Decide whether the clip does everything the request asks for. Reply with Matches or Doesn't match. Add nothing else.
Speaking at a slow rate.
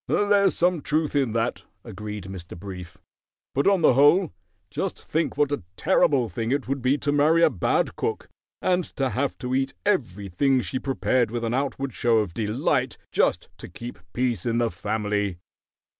Doesn't match